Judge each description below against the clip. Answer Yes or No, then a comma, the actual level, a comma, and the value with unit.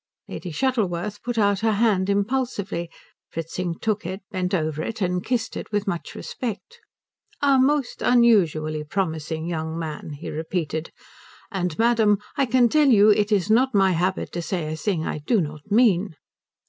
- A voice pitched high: Yes, high, 195 Hz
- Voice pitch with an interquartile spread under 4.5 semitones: No, average, 5.3 semitones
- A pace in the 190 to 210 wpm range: No, average, 165 wpm